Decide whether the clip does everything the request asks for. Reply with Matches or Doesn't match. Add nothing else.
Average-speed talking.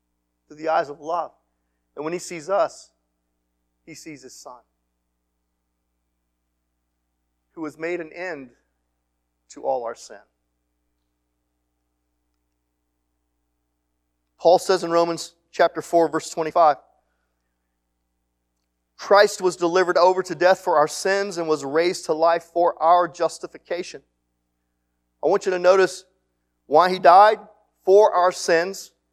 Doesn't match